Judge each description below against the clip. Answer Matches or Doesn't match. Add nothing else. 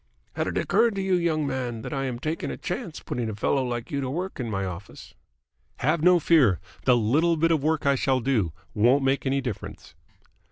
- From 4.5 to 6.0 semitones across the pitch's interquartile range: Matches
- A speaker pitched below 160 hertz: Matches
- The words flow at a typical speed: Doesn't match